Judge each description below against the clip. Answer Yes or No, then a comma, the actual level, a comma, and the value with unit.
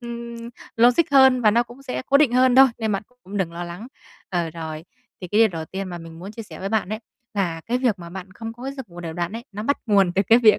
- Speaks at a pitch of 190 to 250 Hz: Yes, high, 210 Hz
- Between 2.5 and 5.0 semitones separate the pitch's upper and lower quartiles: No, wide, 5.4 semitones